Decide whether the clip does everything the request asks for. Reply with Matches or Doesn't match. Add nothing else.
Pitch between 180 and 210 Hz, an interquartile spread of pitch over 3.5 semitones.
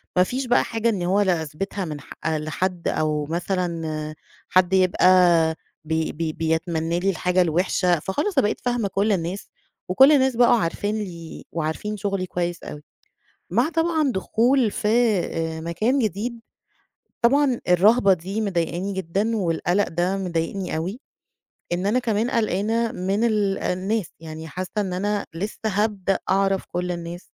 Matches